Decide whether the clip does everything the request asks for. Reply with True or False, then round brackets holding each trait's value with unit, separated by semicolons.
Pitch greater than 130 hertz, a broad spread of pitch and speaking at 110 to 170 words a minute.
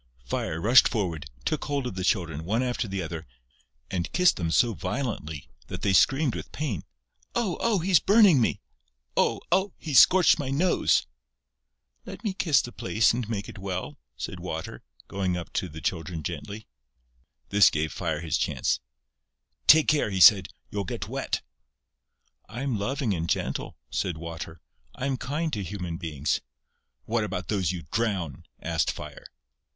False (100 Hz; 8.0 semitones; 165 wpm)